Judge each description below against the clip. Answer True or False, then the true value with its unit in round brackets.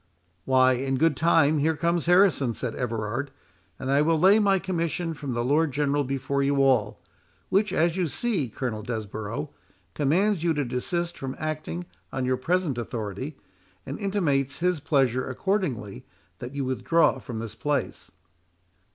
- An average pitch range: True (4.7 semitones)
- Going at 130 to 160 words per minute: True (155 wpm)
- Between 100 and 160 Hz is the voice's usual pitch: True (140 Hz)